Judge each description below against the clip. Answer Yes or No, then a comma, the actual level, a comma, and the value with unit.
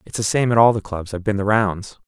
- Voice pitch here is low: Yes, low, 105 Hz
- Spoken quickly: Yes, fast, 315 wpm